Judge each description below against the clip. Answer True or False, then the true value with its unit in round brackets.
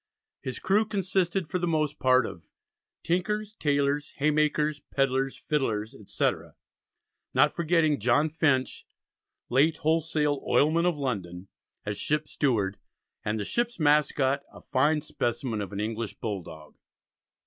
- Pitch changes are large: False (5.0 semitones)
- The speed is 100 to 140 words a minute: True (135 wpm)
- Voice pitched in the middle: True (145 Hz)